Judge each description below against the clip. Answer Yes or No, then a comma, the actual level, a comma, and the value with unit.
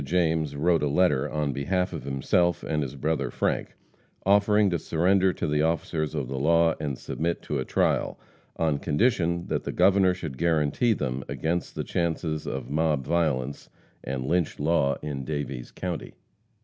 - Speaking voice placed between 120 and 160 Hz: No, very low, 80 Hz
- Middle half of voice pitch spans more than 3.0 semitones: Yes, average, 3.5 semitones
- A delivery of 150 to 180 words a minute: Yes, average, 165 wpm